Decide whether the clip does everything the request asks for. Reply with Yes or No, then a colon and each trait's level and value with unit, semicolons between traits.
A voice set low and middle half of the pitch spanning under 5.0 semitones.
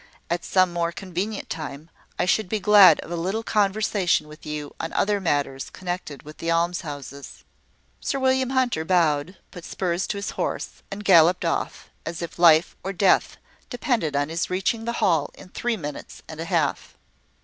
No: medium, 175 Hz; average, 4.0 semitones